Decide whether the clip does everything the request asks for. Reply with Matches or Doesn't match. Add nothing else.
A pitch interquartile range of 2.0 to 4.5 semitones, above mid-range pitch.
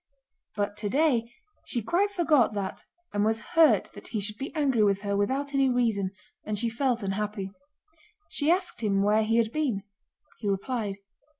Doesn't match